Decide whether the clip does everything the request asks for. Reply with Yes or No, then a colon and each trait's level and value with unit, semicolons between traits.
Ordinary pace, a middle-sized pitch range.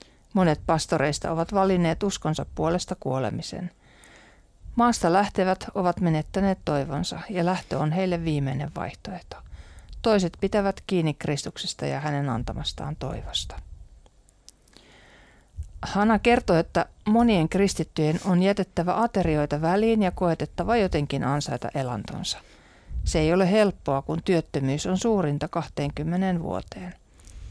Yes: average, 110 wpm; average, 4.9 semitones